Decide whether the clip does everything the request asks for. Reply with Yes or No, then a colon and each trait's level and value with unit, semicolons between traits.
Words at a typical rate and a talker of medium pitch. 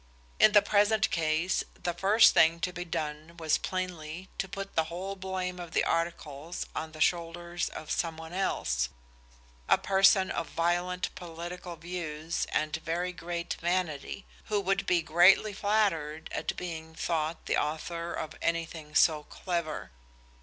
Yes: average, 150 wpm; medium, 170 Hz